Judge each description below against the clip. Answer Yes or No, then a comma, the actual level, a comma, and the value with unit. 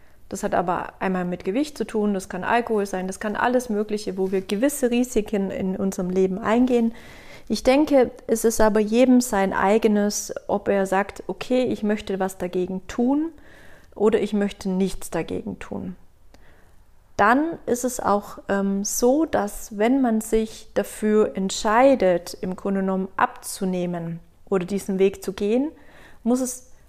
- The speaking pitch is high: Yes, high, 210 Hz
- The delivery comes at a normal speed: Yes, average, 155 wpm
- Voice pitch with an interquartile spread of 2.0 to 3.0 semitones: No, average, 3.9 semitones